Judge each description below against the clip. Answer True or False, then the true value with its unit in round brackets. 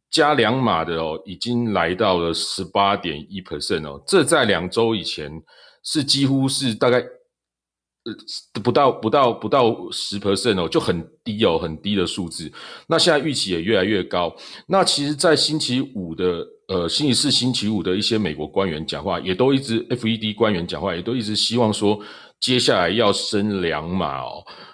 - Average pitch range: False (5.8 semitones)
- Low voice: True (110 Hz)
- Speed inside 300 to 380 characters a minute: False (285 characters per minute)